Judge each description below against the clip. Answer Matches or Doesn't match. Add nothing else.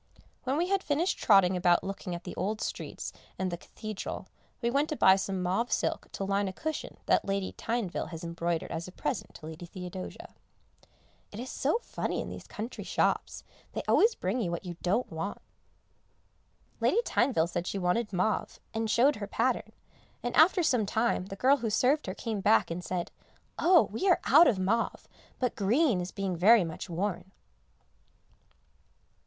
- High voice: Matches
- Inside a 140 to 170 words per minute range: Doesn't match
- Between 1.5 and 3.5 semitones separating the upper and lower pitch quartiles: Doesn't match